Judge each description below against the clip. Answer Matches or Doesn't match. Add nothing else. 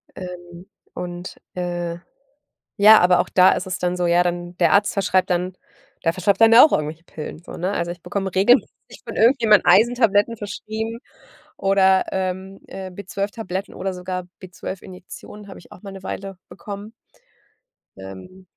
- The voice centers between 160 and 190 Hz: Matches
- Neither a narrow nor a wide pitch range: Doesn't match